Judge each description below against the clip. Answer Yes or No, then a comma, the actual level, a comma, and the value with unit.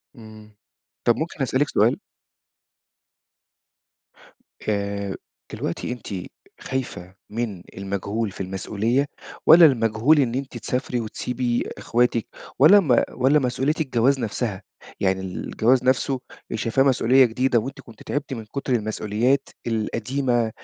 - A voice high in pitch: No, low, 120 Hz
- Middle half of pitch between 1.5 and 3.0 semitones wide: No, average, 3.6 semitones